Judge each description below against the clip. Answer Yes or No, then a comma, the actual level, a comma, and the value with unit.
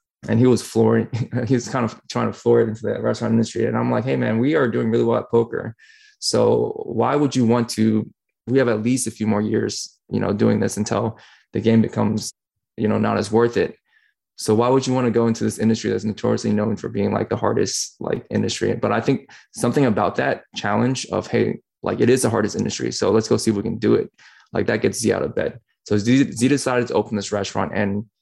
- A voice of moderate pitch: No, low, 115 Hz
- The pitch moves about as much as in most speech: No, narrow, 2.2 semitones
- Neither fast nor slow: No, fast, 245 wpm